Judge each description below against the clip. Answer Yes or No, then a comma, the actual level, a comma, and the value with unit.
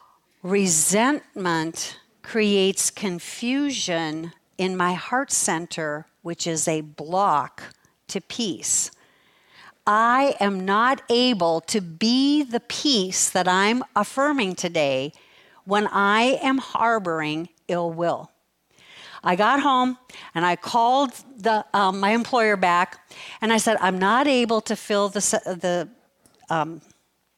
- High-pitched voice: Yes, high, 200 Hz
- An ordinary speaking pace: No, slow, 115 wpm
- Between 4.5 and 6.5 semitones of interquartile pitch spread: Yes, average, 5.1 semitones